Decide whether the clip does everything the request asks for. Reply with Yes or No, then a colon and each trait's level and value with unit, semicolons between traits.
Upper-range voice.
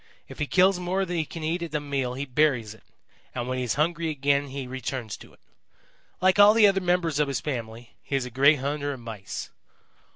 No: medium, 145 Hz